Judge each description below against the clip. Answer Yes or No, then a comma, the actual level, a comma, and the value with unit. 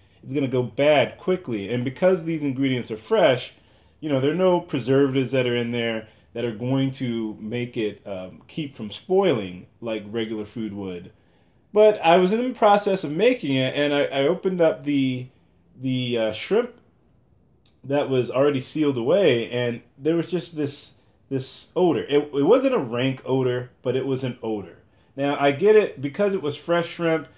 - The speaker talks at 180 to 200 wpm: Yes, average, 185 wpm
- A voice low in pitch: Yes, low, 130 Hz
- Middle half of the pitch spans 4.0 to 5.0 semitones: Yes, average, 4.7 semitones